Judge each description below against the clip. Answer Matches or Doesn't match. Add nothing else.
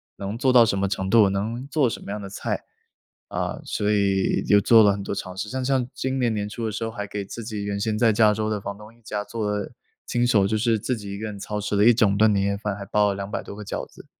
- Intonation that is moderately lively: Doesn't match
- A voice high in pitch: Doesn't match